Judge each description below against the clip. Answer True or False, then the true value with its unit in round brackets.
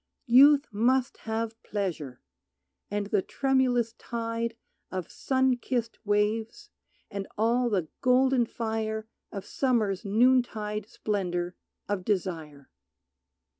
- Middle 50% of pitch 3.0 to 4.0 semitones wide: True (3.5 semitones)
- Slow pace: True (100 wpm)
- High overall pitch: True (220 Hz)